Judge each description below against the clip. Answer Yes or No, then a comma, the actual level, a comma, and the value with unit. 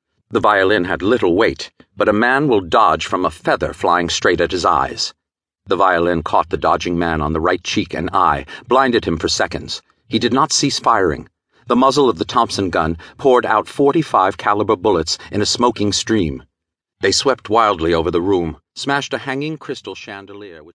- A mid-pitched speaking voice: No, low, 105 Hz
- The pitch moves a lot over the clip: Yes, wide, 6.6 semitones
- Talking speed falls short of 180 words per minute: No, average, 190 wpm